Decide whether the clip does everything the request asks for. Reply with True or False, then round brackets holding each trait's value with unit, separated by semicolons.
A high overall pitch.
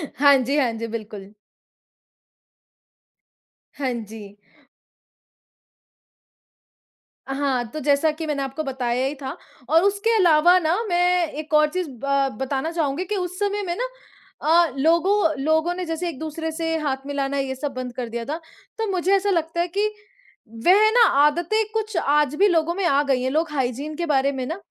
True (310 Hz)